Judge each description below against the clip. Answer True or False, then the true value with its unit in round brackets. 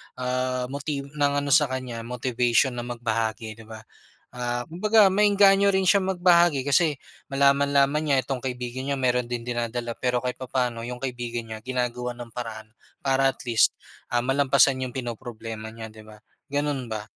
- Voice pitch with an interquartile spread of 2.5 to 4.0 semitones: True (2.9 semitones)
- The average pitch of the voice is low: True (125 Hz)